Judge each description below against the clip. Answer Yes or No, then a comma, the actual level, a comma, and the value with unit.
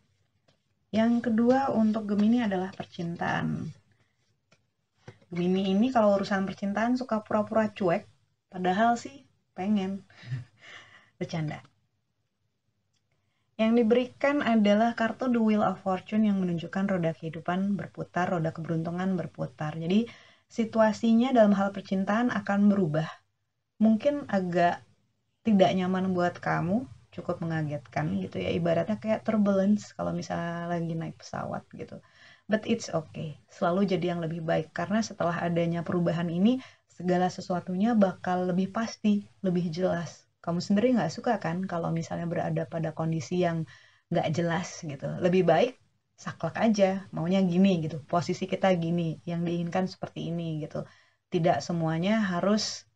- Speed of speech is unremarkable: Yes, average, 125 wpm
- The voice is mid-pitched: Yes, medium, 180 Hz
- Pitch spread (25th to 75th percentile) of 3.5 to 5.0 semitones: Yes, average, 4.0 semitones